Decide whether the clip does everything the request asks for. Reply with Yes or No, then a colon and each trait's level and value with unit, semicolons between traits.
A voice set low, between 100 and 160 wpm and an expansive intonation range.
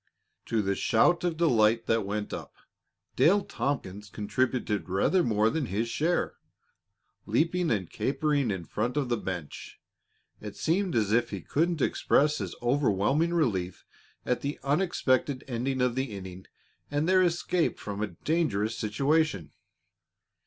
Yes: low, 125 Hz; average, 140 wpm; wide, 7.1 semitones